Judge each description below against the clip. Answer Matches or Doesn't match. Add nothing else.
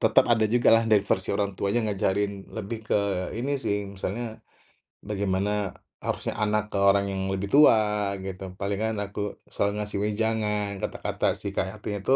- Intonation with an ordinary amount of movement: Doesn't match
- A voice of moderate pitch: Doesn't match